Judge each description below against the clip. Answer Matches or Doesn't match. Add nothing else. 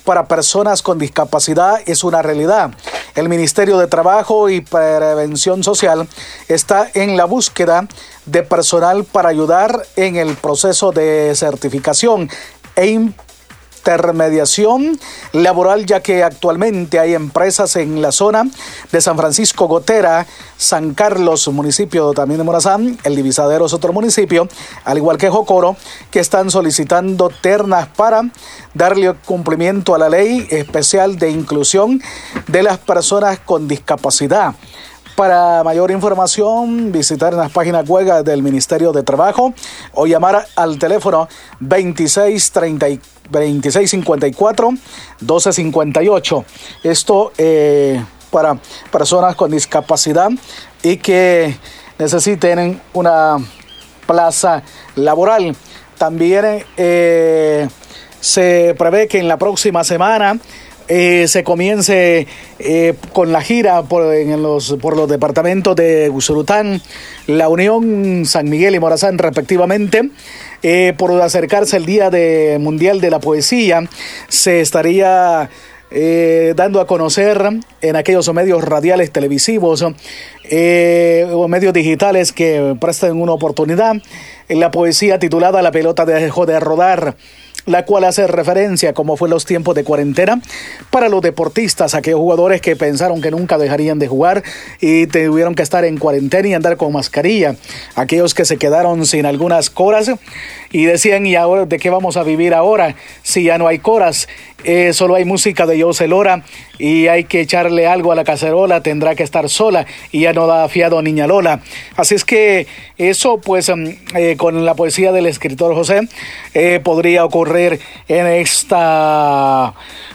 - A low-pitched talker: Doesn't match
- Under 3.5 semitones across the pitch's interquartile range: Matches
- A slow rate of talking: Doesn't match